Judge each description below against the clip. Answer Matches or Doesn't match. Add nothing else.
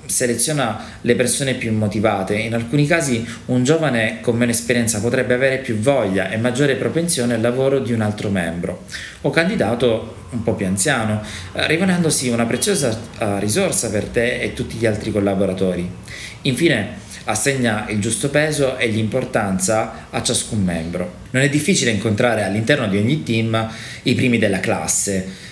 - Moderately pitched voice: Doesn't match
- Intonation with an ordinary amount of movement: Matches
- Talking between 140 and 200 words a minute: Matches